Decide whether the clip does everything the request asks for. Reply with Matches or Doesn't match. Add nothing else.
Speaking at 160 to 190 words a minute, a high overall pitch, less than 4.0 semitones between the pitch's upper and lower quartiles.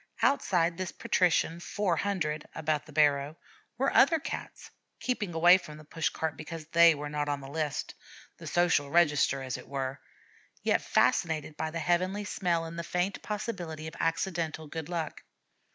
Doesn't match